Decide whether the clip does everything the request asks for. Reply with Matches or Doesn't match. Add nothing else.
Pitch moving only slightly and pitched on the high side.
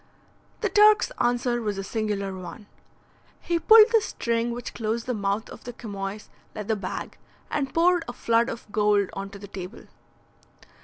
Doesn't match